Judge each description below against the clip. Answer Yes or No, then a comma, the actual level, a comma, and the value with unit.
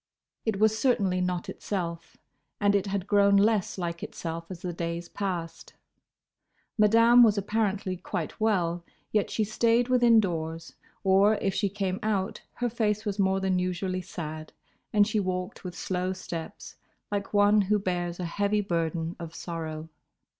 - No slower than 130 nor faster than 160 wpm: Yes, average, 155 wpm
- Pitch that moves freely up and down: No, average, 3.1 semitones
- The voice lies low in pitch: No, high, 190 Hz